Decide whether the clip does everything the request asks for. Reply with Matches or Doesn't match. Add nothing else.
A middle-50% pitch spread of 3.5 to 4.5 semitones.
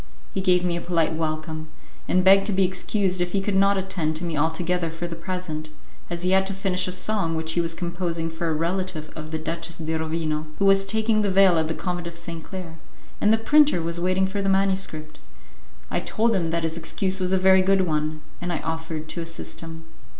Doesn't match